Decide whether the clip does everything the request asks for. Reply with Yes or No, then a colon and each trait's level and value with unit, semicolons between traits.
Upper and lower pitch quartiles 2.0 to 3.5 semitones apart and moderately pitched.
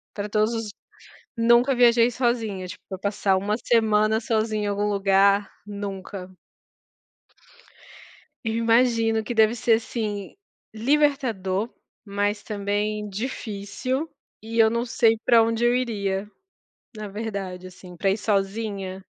No: narrow, 2.5 semitones; high, 215 Hz